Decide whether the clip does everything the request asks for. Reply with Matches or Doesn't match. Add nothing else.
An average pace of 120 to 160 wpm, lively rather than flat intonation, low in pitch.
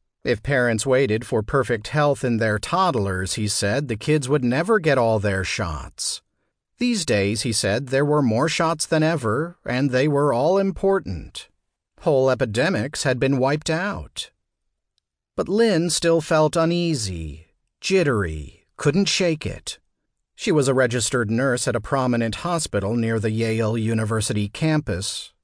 Matches